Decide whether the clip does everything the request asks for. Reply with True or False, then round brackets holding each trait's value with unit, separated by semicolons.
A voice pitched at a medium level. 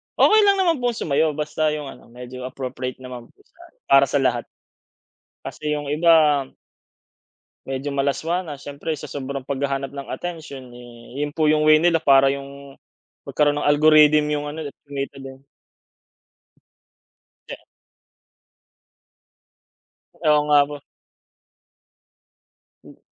True (145 Hz)